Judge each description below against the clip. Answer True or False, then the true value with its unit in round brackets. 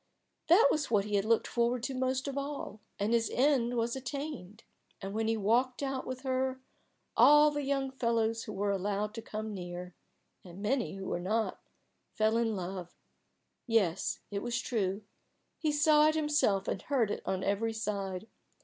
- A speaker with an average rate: True (175 wpm)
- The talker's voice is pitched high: True (230 Hz)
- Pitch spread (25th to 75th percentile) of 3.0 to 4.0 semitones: False (4.6 semitones)